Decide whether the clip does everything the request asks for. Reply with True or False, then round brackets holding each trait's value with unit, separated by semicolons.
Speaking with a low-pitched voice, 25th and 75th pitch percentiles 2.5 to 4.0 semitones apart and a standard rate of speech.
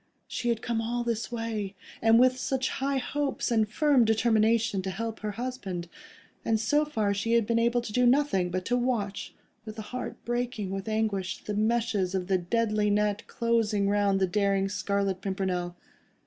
False (220 Hz; 3.1 semitones; 180 wpm)